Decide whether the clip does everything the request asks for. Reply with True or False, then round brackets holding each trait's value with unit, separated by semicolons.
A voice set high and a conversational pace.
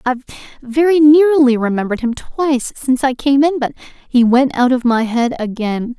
True (260 Hz; 180 wpm)